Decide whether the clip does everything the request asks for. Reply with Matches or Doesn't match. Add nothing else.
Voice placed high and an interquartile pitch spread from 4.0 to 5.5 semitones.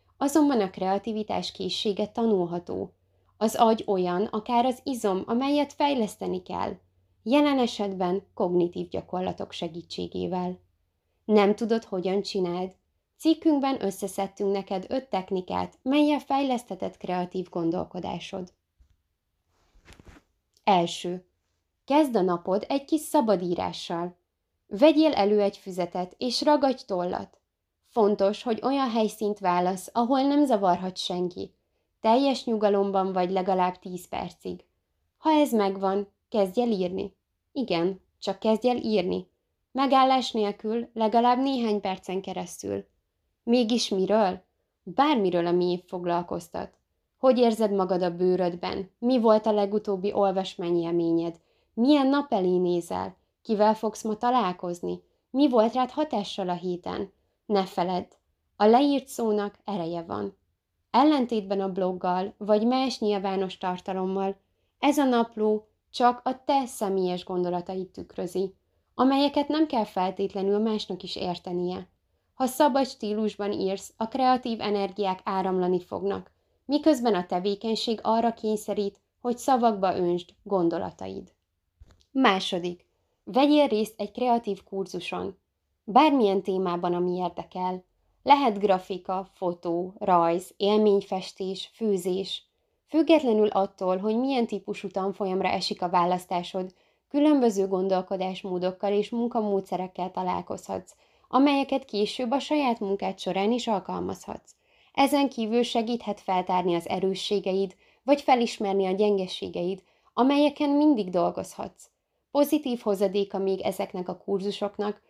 Matches